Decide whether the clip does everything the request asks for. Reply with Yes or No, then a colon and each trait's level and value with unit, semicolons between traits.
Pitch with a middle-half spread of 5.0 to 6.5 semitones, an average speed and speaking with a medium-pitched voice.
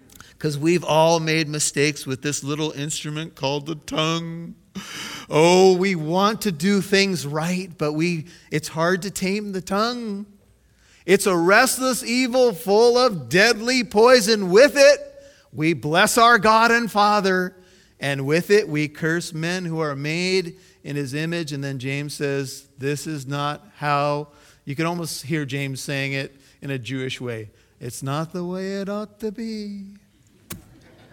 Yes: wide, 5.4 semitones; average, 160 wpm; medium, 165 Hz